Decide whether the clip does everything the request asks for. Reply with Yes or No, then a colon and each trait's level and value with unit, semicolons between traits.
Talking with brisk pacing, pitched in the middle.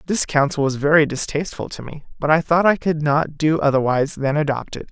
Yes: fast, 220 wpm; medium, 150 Hz